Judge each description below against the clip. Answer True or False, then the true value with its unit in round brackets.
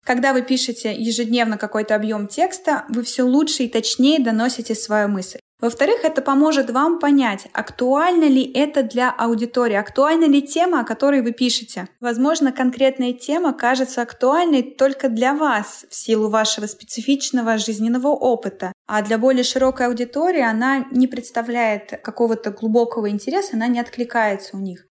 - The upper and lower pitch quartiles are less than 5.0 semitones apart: True (3.4 semitones)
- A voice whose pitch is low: False (245 Hz)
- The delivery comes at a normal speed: True (150 wpm)